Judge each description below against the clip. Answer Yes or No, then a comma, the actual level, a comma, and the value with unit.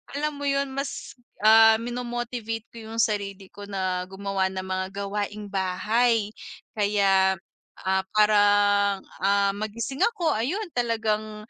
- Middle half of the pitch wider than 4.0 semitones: No, average, 2.8 semitones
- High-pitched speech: Yes, high, 210 Hz